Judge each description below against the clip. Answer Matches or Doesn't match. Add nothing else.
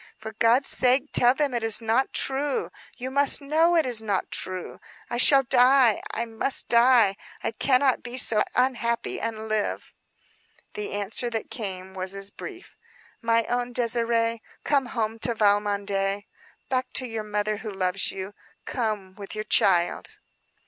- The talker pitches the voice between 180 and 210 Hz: Doesn't match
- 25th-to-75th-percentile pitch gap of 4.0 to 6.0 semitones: Doesn't match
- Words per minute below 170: Matches